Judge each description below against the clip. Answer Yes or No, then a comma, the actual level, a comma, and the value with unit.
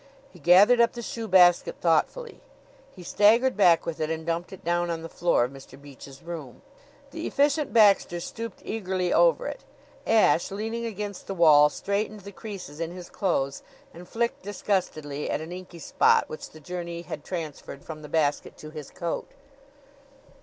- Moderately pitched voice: Yes, medium, 175 Hz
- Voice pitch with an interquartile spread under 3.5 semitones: No, average, 4.8 semitones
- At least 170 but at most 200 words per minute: Yes, average, 175 wpm